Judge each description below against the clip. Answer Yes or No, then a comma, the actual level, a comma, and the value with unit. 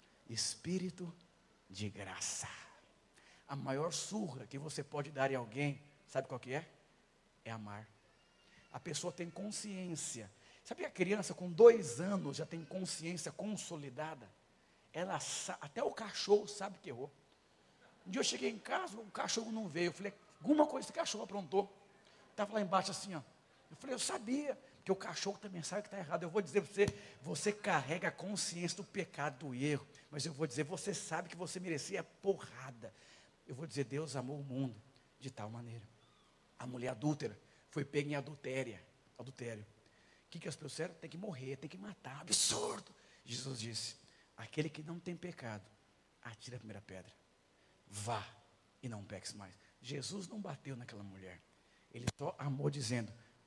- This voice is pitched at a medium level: Yes, medium, 150 Hz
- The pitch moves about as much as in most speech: No, wide, 7.2 semitones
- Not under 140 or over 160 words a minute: No, average, 170 wpm